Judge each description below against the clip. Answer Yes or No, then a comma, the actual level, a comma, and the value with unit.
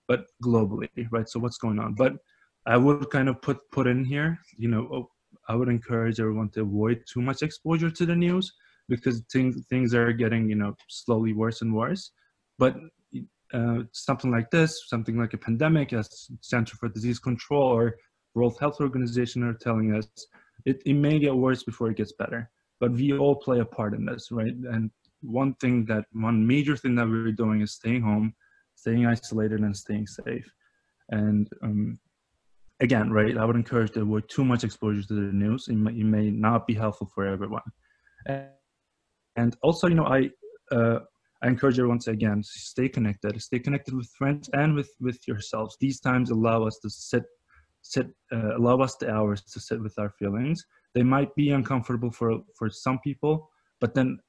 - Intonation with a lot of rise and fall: No, average, 3.2 semitones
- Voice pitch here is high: No, low, 120 Hz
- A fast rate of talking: No, average, 190 wpm